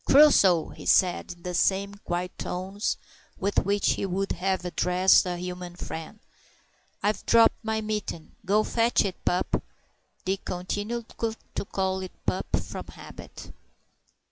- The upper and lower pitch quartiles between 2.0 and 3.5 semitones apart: Yes, narrow, 2.6 semitones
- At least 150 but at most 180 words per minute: No, average, 140 wpm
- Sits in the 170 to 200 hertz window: Yes, high, 190 Hz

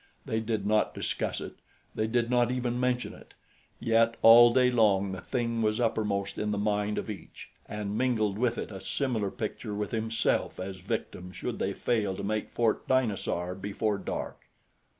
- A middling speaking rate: Yes, average, 175 wpm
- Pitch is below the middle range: Yes, low, 110 Hz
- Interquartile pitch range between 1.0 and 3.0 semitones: Yes, narrow, 2.6 semitones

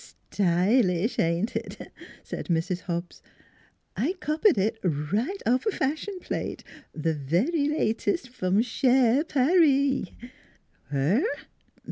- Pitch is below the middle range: No, high, 230 Hz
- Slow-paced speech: Yes, slow, 105 wpm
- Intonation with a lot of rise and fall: Yes, wide, 8.2 semitones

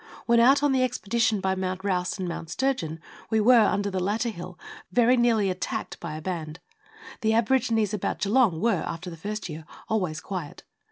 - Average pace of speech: Yes, average, 185 wpm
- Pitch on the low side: No, high, 205 Hz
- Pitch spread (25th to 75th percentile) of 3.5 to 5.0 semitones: Yes, average, 4.5 semitones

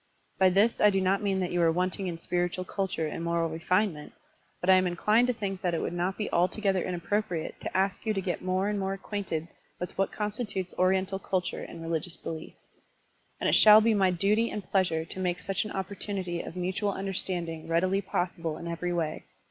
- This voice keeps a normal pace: No, fast, 210 wpm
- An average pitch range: No, narrow, 2.3 semitones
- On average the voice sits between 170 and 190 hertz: Yes, medium, 185 Hz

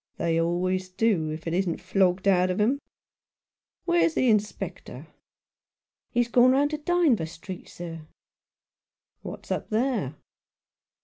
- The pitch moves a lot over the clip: Yes, wide, 6.2 semitones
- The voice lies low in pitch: No, high, 190 Hz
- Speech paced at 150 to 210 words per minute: No, slow, 135 wpm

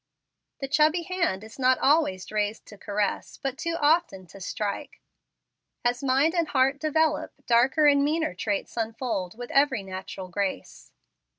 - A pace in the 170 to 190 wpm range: No, average, 150 wpm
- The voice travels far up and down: Yes, wide, 6.8 semitones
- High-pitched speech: Yes, very high, 255 Hz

